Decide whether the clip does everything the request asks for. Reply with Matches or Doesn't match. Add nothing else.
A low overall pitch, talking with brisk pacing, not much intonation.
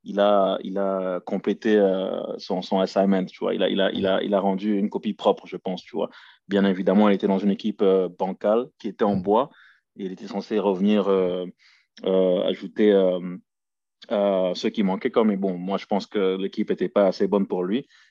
Matches